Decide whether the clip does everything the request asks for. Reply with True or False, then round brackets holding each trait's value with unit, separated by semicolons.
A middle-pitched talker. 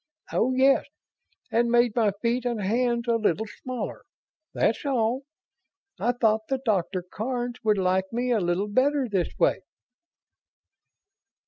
False (235 Hz)